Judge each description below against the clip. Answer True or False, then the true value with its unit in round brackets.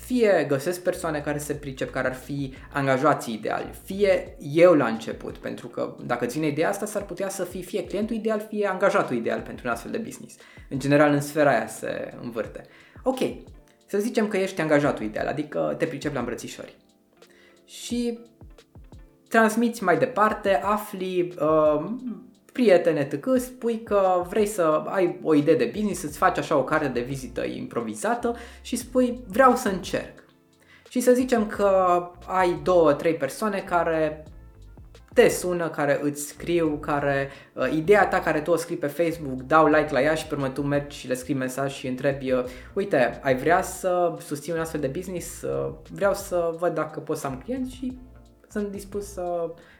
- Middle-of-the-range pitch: True (175 Hz)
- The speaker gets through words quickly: True (175 wpm)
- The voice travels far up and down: True (5.9 semitones)